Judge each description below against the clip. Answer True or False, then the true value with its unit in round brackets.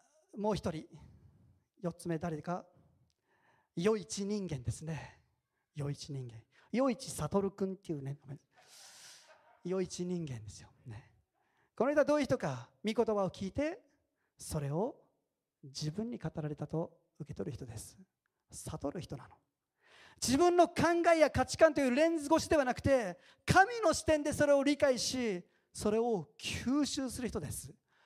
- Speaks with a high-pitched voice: True (200 Hz)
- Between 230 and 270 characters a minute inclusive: True (265 characters per minute)